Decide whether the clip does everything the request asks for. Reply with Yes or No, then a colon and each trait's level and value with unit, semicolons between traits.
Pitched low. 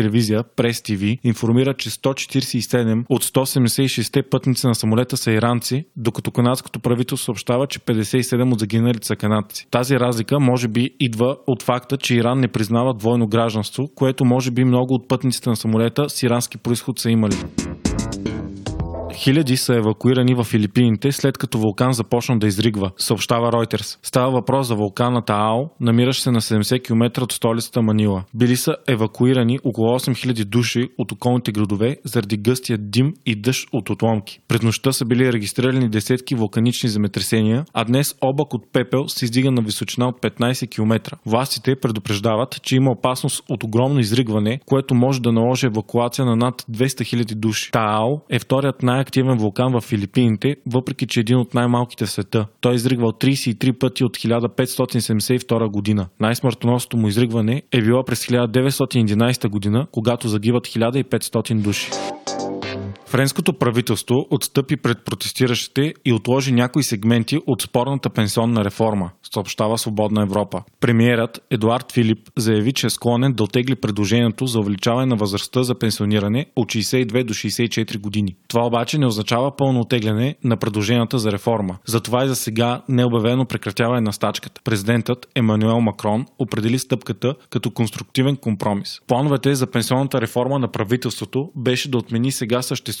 Yes: low, 120 Hz